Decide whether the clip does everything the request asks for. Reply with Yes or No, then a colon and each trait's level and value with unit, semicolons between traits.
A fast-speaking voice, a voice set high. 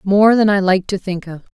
Yes: fast, 270 wpm; high, 195 Hz